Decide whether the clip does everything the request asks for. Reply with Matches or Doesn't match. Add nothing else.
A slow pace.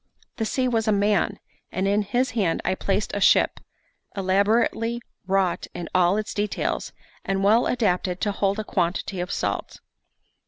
Doesn't match